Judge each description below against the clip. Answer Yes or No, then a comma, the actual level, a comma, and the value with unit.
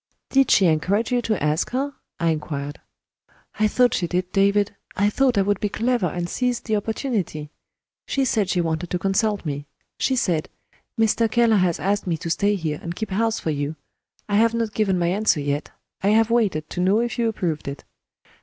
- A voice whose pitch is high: Yes, high, 200 Hz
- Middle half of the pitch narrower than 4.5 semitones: No, average, 5.0 semitones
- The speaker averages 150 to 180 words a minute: No, average, 200 wpm